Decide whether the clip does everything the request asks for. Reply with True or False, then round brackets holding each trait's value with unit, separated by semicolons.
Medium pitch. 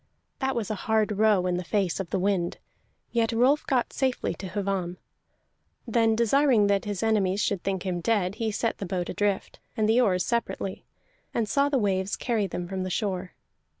False (205 Hz)